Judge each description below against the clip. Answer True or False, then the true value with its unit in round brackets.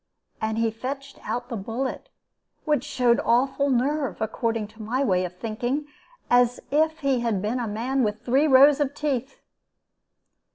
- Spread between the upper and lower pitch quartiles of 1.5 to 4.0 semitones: True (3.5 semitones)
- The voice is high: True (245 Hz)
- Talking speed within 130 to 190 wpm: True (160 wpm)